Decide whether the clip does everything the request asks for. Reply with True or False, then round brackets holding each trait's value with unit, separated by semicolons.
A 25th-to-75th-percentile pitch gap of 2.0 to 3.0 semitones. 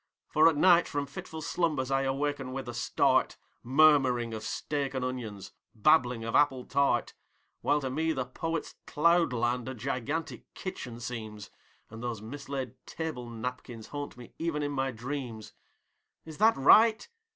False (3.6 semitones)